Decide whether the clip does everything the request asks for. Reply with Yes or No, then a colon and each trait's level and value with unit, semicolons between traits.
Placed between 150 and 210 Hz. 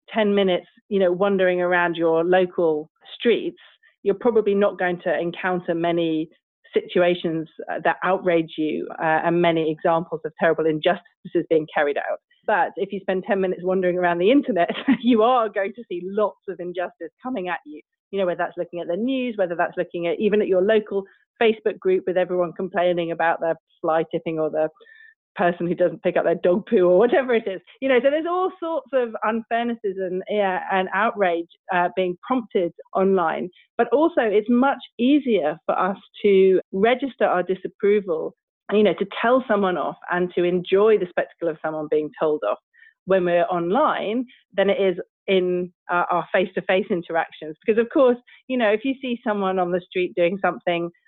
Yes: medium, 185 Hz